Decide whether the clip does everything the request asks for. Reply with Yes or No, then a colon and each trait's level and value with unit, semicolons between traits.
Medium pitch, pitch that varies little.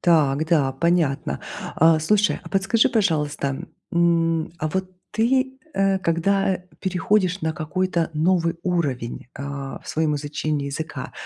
No: medium, 165 Hz; average, 3.8 semitones